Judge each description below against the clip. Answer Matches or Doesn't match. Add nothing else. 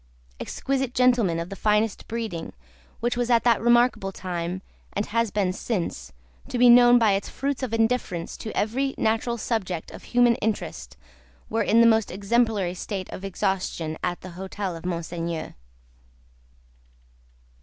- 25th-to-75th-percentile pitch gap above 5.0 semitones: Doesn't match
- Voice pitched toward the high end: Matches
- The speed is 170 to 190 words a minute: Doesn't match